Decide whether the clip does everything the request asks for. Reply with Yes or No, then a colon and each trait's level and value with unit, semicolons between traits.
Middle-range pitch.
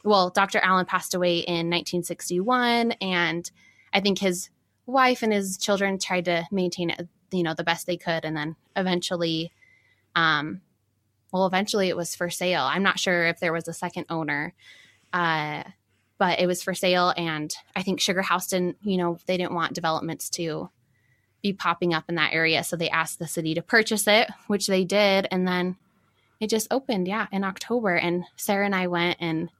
Yes: medium, 180 Hz